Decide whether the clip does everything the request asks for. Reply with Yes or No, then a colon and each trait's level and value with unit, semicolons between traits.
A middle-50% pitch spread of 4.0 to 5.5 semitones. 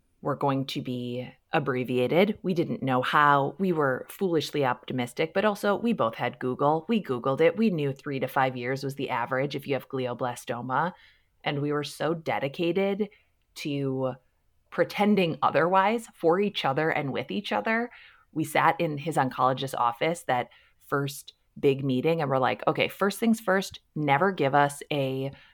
Yes: average, 4.7 semitones